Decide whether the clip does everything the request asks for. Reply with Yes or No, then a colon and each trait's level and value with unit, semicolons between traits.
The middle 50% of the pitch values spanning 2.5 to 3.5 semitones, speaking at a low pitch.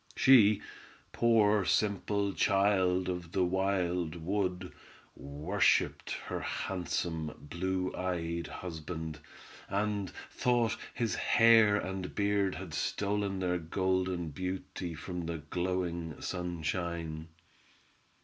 Yes: average, 2.9 semitones; very low, 90 Hz